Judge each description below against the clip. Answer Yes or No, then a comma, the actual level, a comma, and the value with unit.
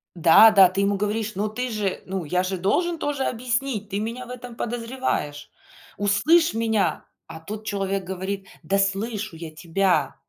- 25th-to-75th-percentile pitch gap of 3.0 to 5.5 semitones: Yes, average, 3.5 semitones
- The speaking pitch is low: No, high, 205 Hz